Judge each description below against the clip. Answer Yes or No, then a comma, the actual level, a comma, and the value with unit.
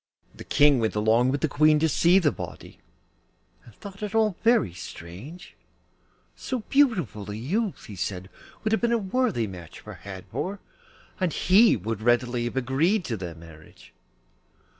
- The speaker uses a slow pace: No, average, 160 wpm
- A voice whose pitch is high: No, medium, 140 Hz